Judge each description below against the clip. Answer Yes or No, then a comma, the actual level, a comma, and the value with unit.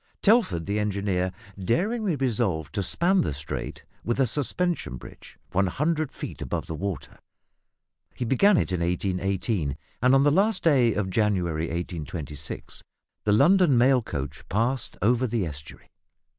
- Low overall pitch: Yes, low, 105 Hz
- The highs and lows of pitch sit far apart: Yes, wide, 7.8 semitones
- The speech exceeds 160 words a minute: No, average, 145 wpm